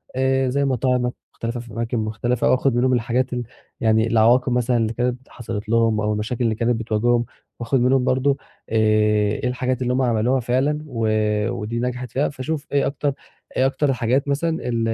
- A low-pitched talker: Yes, low, 125 Hz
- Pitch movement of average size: No, narrow, 2.3 semitones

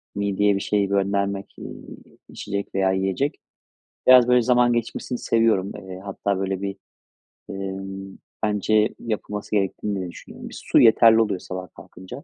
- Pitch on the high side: No, low, 100 Hz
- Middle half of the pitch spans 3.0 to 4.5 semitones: No, narrow, 2.4 semitones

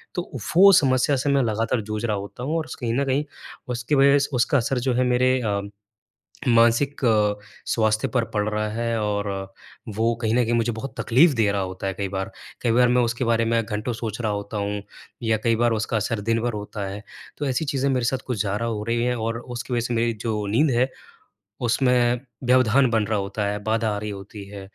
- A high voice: No, low, 115 Hz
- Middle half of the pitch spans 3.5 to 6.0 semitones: No, average, 2.9 semitones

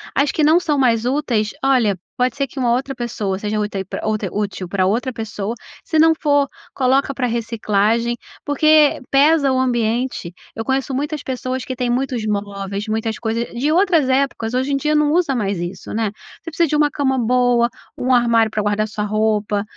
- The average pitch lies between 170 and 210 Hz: No, high, 245 Hz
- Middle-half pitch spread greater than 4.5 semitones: No, average, 4.2 semitones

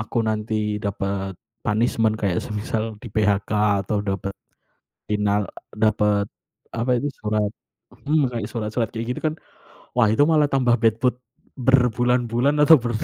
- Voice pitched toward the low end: Yes, low, 110 Hz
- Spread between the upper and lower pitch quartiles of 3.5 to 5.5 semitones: No, average, 2.8 semitones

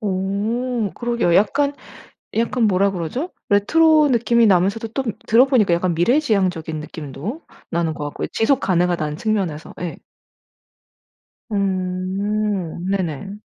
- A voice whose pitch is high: Yes, high, 200 Hz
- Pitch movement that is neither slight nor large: Yes, average, 5.0 semitones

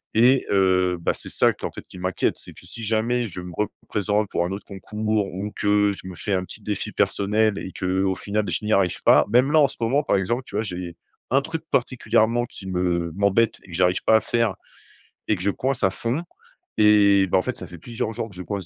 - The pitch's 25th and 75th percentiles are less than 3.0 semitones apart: No, average, 3.3 semitones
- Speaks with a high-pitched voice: No, low, 105 Hz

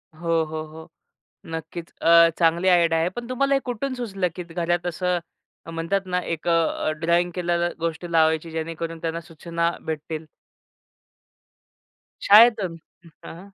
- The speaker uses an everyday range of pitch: No, narrow, 1.8 semitones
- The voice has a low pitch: No, medium, 170 Hz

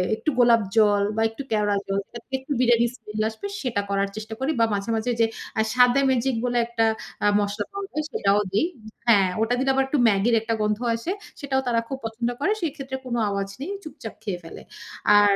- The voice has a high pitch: Yes, high, 230 Hz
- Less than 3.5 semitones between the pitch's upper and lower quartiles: No, average, 4.2 semitones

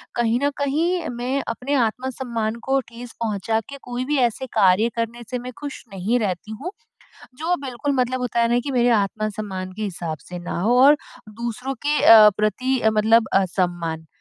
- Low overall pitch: No, high, 235 Hz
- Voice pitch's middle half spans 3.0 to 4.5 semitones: Yes, average, 3.6 semitones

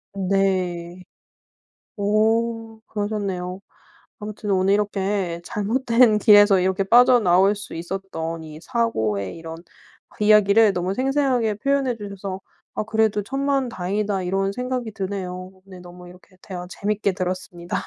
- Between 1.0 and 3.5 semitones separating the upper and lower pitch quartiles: Yes, average, 3.2 semitones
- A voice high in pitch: Yes, high, 200 Hz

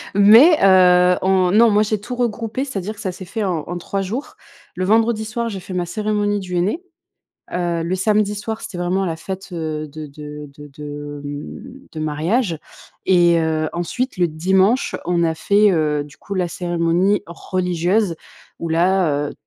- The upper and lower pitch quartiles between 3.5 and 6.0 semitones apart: Yes, average, 4.0 semitones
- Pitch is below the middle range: No, medium, 180 Hz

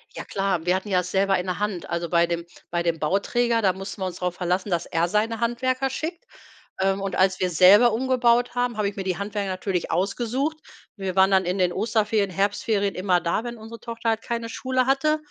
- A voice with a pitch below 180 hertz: No, high, 200 Hz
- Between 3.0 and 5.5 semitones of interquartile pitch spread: Yes, average, 4.2 semitones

